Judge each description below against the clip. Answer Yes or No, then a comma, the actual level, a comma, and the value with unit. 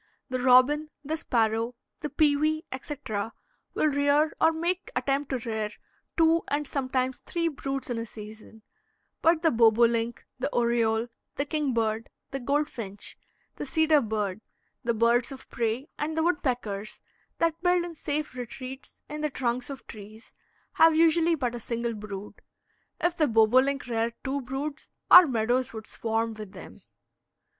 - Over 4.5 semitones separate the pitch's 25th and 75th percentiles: Yes, average, 5.0 semitones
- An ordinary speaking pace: Yes, average, 150 wpm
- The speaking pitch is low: No, very high, 255 Hz